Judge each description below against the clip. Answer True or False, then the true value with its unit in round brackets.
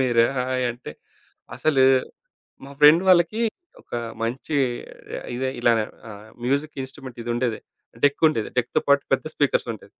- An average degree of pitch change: True (3.2 semitones)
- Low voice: True (130 Hz)